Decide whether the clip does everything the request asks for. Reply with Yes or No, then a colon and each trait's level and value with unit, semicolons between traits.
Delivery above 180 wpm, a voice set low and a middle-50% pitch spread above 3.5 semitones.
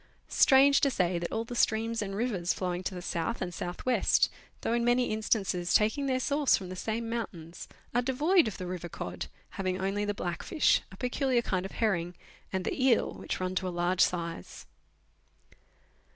No: average, 190 wpm; high, 200 Hz; average, 5.0 semitones